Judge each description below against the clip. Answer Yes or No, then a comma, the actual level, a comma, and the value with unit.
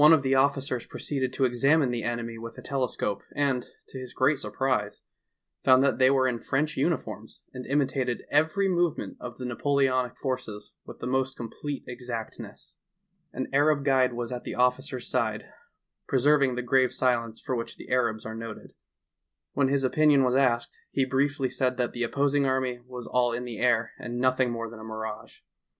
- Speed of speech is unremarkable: Yes, average, 180 wpm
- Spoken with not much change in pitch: Yes, narrow, 2.3 semitones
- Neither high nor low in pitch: No, low, 130 Hz